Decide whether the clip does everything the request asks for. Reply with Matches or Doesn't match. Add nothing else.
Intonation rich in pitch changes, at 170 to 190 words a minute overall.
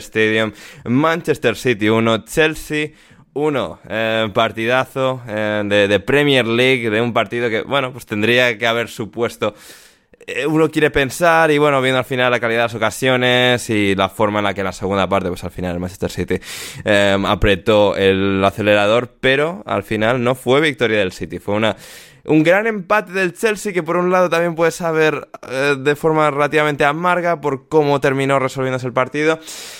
Matches